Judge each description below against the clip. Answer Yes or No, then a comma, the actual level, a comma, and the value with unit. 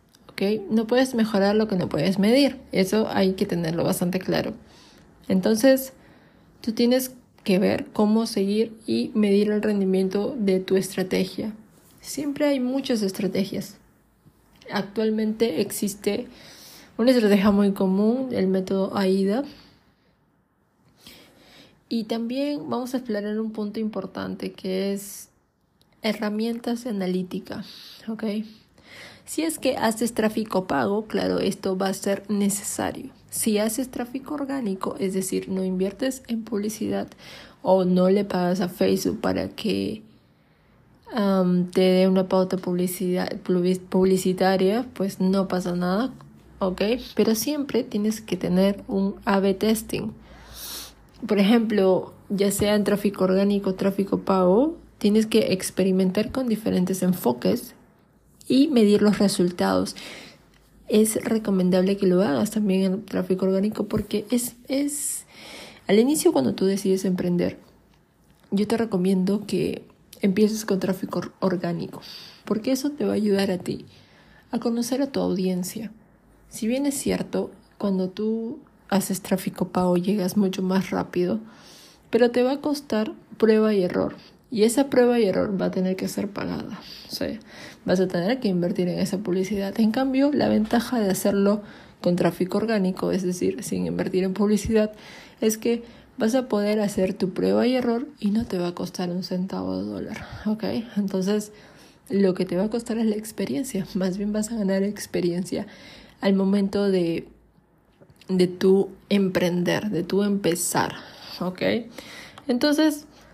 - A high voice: Yes, high, 205 Hz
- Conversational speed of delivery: Yes, average, 140 wpm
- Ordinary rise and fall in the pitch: Yes, average, 3.1 semitones